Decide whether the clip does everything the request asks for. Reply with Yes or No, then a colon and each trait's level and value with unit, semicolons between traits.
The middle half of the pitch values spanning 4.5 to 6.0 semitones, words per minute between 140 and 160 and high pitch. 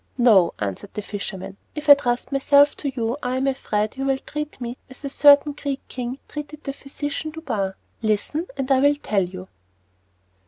No: average, 5.0 semitones; average, 185 wpm; very high, 265 Hz